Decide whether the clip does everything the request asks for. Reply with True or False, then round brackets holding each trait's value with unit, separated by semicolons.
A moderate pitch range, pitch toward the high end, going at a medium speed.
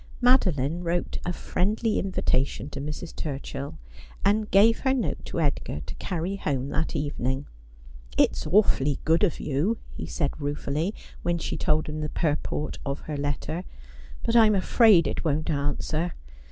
False (5.0 semitones; 155 Hz; 155 wpm)